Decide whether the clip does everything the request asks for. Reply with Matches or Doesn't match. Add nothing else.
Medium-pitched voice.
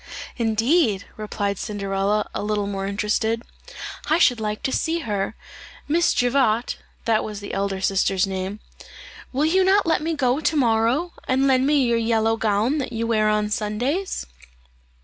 Doesn't match